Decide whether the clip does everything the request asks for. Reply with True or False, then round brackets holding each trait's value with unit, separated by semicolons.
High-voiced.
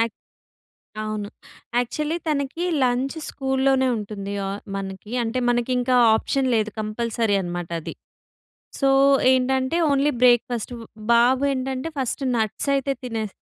True (245 Hz)